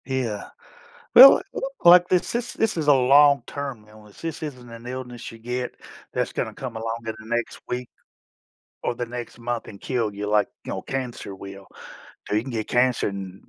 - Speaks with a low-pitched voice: Yes, low, 120 Hz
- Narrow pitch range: No, average, 3.5 semitones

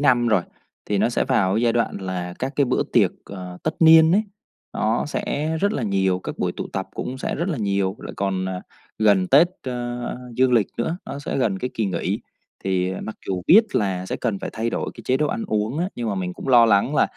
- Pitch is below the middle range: Yes, low, 115 Hz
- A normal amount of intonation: No, wide, 5.7 semitones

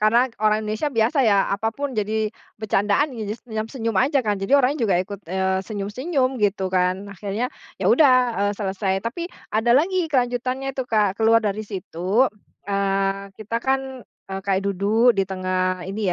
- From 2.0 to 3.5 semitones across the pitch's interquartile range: No, average, 4.3 semitones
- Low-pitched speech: No, high, 215 Hz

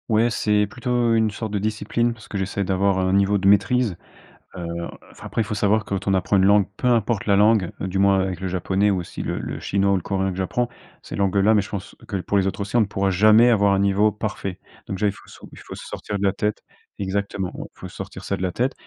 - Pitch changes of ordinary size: No, narrow, 1.9 semitones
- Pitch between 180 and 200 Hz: No, low, 100 Hz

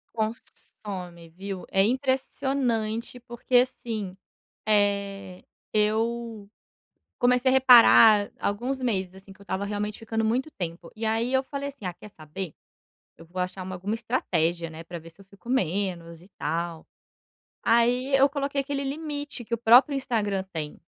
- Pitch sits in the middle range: No, high, 215 Hz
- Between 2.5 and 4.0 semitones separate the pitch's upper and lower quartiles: No, average, 5.0 semitones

